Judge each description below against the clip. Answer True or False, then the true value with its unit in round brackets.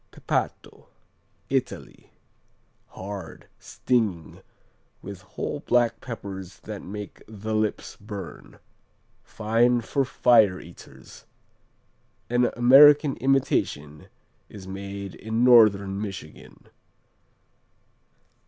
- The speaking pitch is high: False (105 Hz)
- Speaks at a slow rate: True (80 wpm)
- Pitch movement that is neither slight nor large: True (3.7 semitones)